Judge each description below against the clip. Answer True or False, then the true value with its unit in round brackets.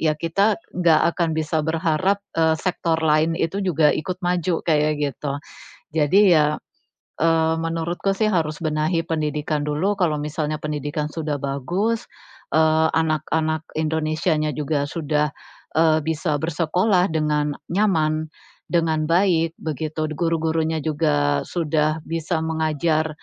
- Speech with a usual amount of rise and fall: False (1.5 semitones)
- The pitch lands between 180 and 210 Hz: False (160 Hz)